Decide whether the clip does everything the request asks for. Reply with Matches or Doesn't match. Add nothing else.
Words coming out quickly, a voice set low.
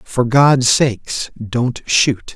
Doesn't match